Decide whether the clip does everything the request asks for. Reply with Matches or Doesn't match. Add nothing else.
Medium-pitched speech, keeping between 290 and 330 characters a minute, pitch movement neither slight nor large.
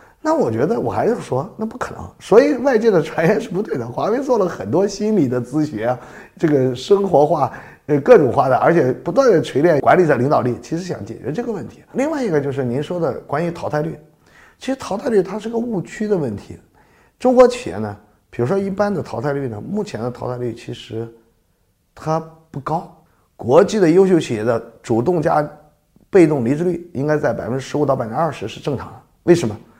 Doesn't match